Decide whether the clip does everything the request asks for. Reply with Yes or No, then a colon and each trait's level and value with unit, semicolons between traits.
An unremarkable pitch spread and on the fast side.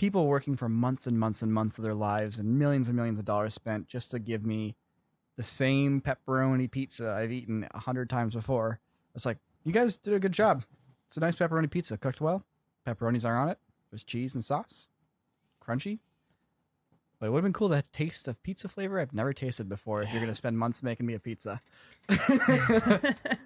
No: wide, 5.9 semitones; fast, 210 wpm